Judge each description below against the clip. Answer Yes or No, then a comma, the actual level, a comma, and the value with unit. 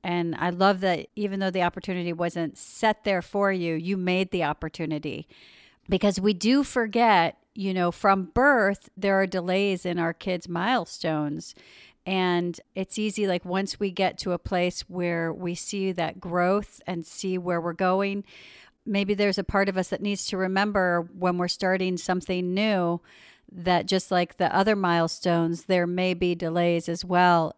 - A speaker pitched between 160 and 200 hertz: Yes, medium, 185 Hz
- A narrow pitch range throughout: Yes, narrow, 2.2 semitones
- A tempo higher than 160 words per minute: Yes, average, 170 wpm